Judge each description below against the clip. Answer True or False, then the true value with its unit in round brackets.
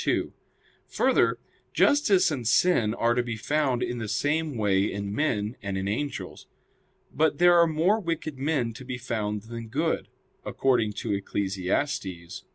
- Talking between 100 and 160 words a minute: True (155 wpm)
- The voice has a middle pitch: False (120 Hz)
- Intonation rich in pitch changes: True (6.6 semitones)